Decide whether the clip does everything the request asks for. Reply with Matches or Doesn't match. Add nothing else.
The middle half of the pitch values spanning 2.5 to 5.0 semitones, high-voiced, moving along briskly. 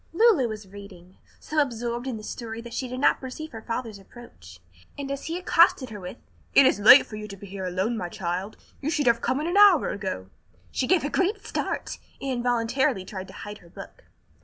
Doesn't match